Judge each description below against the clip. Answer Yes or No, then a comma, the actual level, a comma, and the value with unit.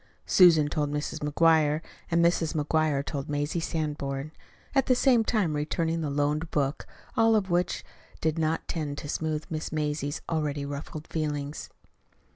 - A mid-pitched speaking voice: Yes, medium, 155 Hz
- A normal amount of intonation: No, narrow, 2.0 semitones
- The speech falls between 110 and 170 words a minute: Yes, average, 150 wpm